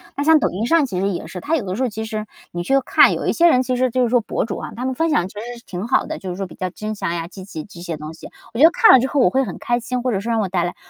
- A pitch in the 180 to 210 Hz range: No, high, 225 Hz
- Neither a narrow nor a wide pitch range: No, wide, 5.7 semitones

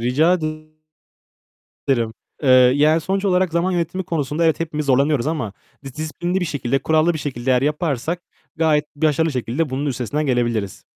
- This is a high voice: No, medium, 150 Hz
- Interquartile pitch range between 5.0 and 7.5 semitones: No, average, 4.0 semitones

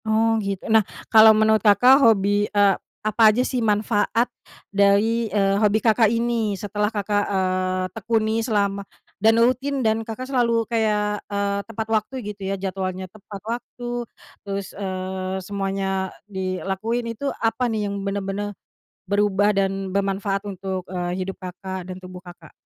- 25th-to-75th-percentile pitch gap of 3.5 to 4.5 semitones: No, narrow, 2.4 semitones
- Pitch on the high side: Yes, high, 205 Hz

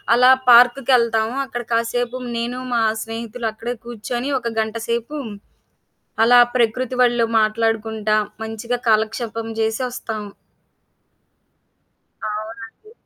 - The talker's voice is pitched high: Yes, high, 230 Hz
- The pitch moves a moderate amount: No, narrow, 1.6 semitones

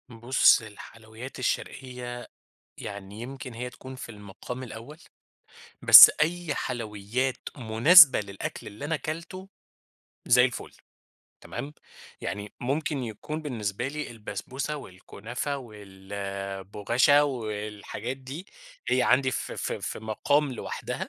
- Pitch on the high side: No, low, 120 Hz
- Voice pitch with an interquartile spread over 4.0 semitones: Yes, average, 4.5 semitones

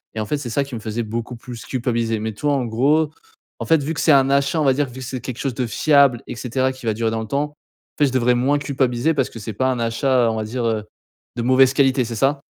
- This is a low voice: Yes, low, 130 Hz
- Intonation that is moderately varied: Yes, average, 3.1 semitones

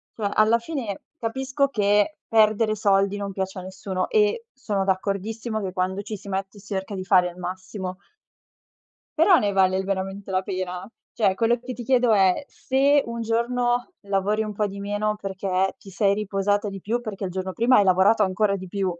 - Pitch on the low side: No, high, 200 Hz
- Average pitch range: Yes, average, 3.0 semitones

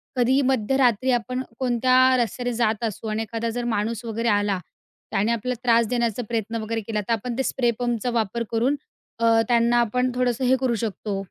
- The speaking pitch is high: Yes, high, 235 Hz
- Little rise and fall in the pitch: Yes, narrow, 1.9 semitones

